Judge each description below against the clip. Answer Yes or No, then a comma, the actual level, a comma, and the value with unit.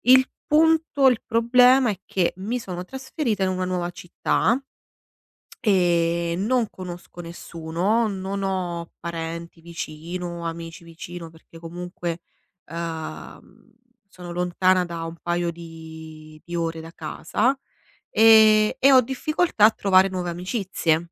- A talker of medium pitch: Yes, medium, 180 Hz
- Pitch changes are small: No, average, 4.3 semitones